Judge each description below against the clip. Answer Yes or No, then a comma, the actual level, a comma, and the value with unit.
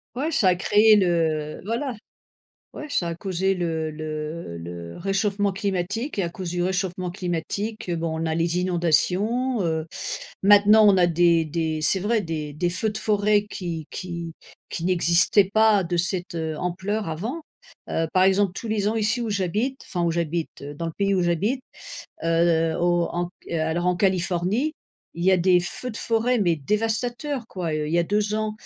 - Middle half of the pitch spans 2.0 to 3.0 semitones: No, average, 3.8 semitones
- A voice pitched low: No, medium, 180 Hz